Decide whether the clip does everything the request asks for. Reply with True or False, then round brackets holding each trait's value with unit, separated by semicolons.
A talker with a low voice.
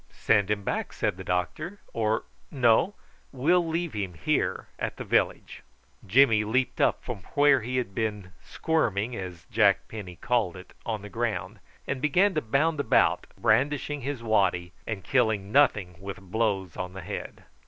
True (110 Hz)